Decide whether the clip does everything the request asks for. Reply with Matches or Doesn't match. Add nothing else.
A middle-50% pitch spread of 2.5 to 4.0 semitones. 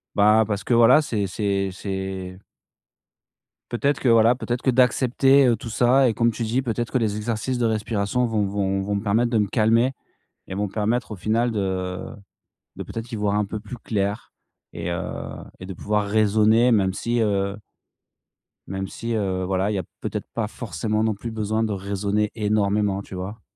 Matches